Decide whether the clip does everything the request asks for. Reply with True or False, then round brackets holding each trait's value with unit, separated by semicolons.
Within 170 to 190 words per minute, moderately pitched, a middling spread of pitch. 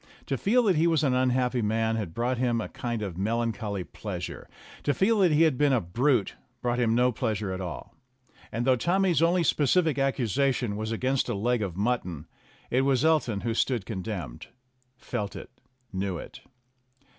False (180 wpm; 120 Hz; 4.5 semitones)